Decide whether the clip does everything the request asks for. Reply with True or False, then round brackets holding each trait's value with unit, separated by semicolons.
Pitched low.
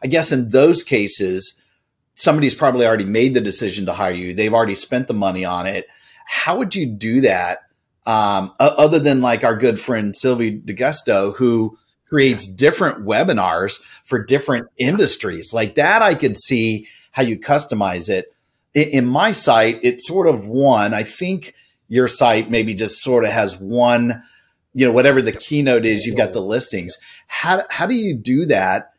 True (120 Hz)